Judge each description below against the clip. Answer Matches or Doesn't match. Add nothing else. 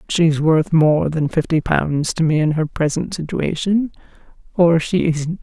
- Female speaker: Matches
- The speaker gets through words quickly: Doesn't match